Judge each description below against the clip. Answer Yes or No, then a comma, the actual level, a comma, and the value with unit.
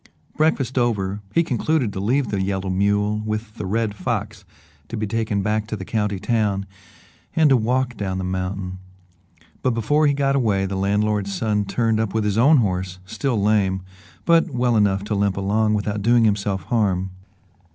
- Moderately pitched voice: No, low, 105 Hz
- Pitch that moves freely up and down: No, average, 3.0 semitones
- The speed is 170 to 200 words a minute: Yes, average, 180 wpm